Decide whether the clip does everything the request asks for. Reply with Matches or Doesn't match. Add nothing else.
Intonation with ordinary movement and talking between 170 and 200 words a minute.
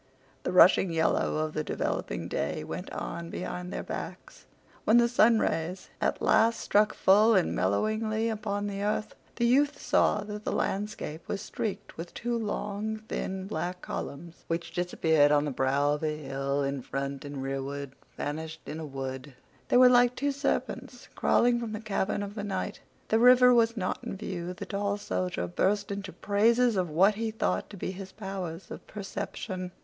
Doesn't match